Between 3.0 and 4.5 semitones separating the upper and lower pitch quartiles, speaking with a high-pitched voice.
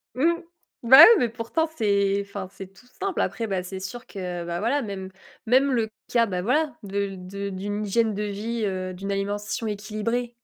Yes: average, 3.3 semitones; high, 205 Hz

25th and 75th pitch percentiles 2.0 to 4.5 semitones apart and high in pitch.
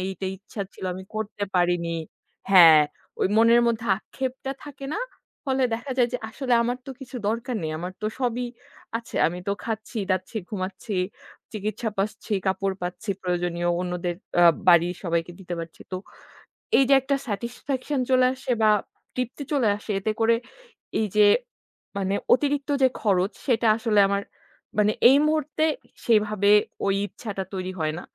No: average, 5.0 semitones; high, 215 Hz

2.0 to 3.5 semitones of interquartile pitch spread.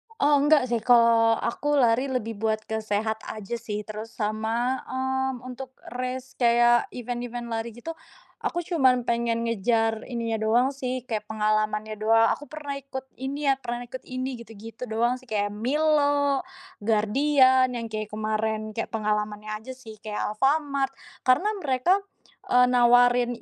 Yes: average, 2.9 semitones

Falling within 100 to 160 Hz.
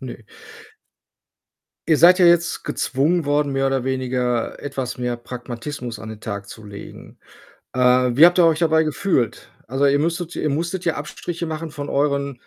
Yes: medium, 140 Hz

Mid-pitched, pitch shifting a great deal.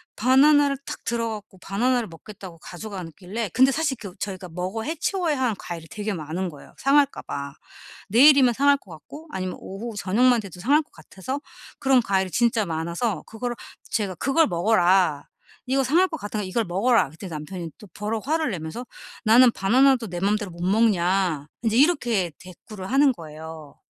No: high, 210 Hz; wide, 6.0 semitones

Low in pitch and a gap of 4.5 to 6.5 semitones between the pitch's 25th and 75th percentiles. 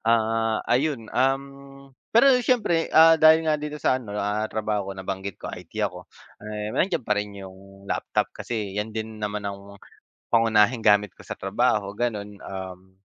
Yes: low, 110 Hz; average, 4.9 semitones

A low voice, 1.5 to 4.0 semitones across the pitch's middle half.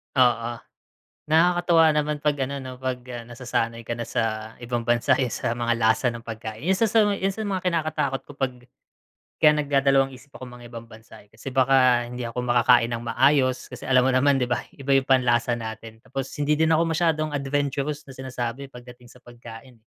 Yes: low, 130 Hz; average, 3.3 semitones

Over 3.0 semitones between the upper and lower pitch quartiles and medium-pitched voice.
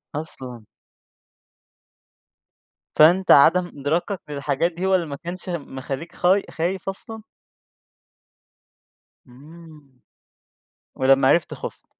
Yes: average, 4.3 semitones; medium, 160 Hz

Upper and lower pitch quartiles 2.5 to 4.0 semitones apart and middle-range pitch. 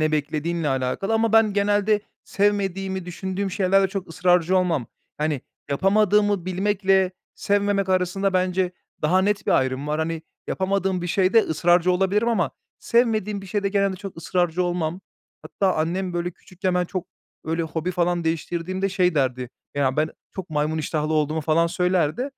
Yes: average, 3.3 semitones; medium, 180 Hz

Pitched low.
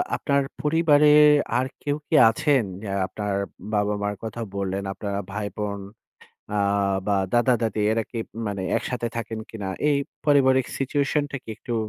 Yes: low, 115 Hz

